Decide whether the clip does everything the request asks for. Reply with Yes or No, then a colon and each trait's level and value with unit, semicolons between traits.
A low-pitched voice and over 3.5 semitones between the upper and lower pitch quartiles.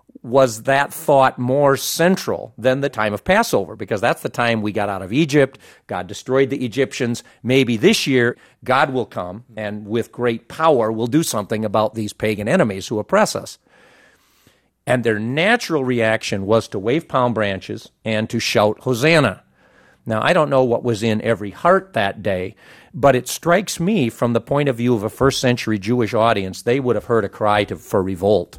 Yes: low, 120 Hz; average, 4.0 semitones